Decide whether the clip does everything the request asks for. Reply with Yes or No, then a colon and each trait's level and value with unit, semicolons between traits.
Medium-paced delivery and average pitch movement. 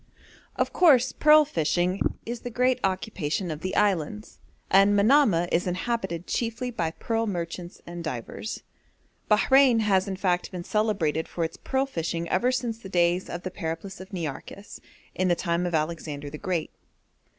Yes: average, 160 wpm; average, 4.9 semitones